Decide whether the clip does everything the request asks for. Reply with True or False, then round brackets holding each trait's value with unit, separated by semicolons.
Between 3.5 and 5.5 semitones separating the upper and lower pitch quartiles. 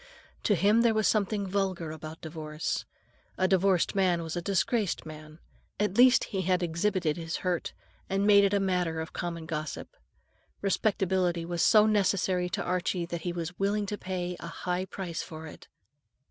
False (3.0 semitones)